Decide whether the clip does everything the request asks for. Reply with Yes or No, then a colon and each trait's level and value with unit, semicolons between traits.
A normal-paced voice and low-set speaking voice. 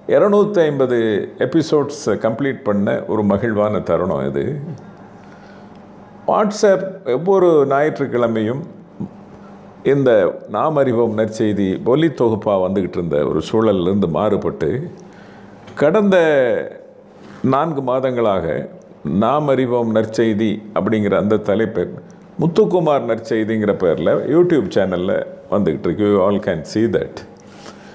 Yes: average, 90 wpm; low, 130 Hz